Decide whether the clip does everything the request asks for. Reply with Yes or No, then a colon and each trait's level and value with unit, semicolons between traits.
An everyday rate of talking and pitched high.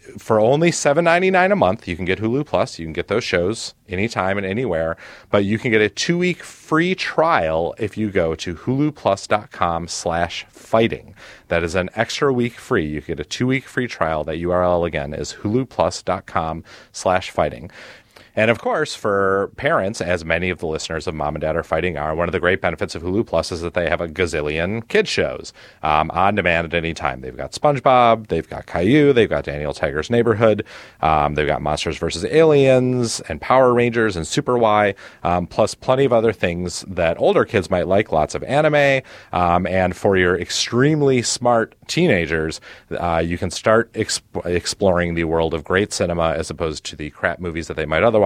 No: average, 195 wpm; very low, 95 Hz